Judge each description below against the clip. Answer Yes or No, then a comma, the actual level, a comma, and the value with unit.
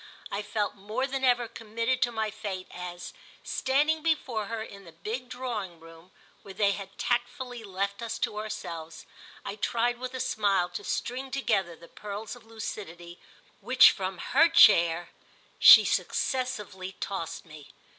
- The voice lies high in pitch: Yes, high, 215 Hz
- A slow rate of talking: No, average, 155 wpm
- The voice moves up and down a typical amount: Yes, average, 4.7 semitones